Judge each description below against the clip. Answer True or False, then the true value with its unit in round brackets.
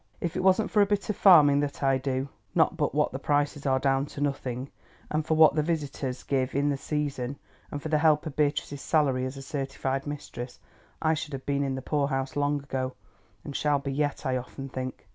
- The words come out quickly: True (220 wpm)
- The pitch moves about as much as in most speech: False (2.0 semitones)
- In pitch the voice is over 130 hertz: True (140 Hz)